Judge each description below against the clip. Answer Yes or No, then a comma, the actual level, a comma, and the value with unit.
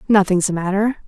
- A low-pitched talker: No, high, 195 Hz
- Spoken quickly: No, average, 170 wpm